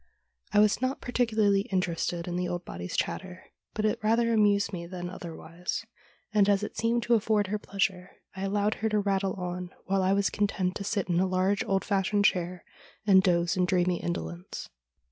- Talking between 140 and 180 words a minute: No, average, 195 wpm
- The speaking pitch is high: Yes, high, 195 Hz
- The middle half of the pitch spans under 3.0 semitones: Yes, narrow, 2.6 semitones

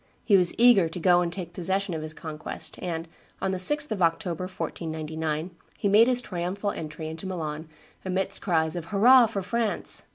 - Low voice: No, medium, 180 Hz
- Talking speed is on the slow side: No, average, 185 wpm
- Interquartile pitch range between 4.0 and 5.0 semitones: No, average, 3.6 semitones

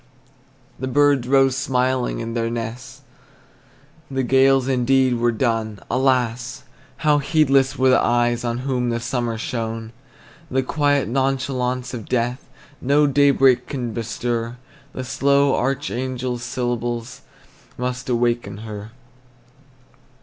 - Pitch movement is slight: Yes, narrow, 2.0 semitones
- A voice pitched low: Yes, low, 125 Hz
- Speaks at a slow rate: Yes, slow, 115 wpm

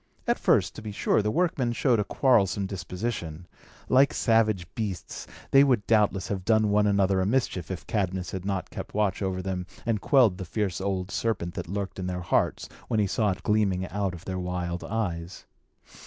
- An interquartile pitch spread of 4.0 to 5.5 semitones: No, average, 2.9 semitones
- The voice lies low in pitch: Yes, low, 100 Hz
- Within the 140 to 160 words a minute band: No, average, 195 wpm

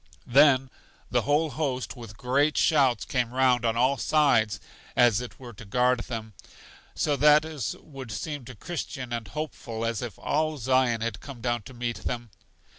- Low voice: Yes, low, 125 Hz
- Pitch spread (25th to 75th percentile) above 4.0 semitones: No, average, 3.4 semitones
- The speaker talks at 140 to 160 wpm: No, average, 175 wpm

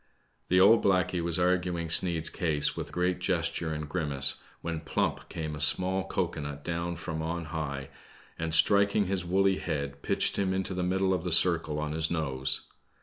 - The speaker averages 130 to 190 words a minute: Yes, average, 180 wpm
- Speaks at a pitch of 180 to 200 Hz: No, very low, 85 Hz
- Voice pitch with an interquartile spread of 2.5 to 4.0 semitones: Yes, average, 2.8 semitones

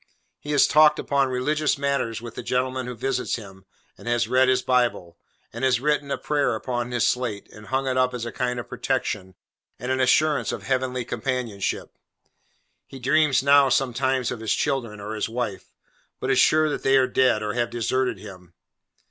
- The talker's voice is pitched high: No, low, 125 Hz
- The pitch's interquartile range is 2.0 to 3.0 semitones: Yes, narrow, 2.4 semitones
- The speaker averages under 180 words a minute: No, average, 190 wpm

